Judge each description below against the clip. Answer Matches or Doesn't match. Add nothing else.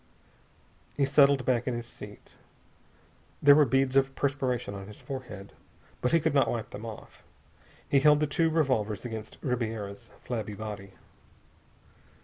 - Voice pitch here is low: Matches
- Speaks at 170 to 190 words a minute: Doesn't match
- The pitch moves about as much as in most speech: Matches